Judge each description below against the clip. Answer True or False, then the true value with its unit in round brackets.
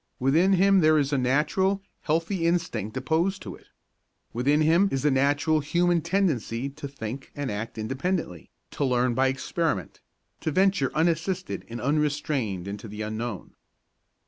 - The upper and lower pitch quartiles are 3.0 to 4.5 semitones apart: False (5.3 semitones)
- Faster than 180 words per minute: False (145 wpm)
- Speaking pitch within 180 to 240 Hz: False (145 Hz)